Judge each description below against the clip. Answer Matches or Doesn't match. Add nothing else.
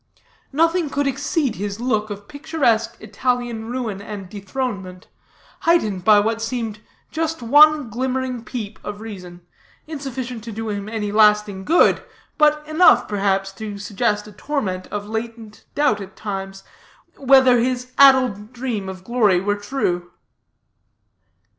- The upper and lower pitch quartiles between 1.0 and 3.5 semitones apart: Doesn't match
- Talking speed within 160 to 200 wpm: Doesn't match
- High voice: Matches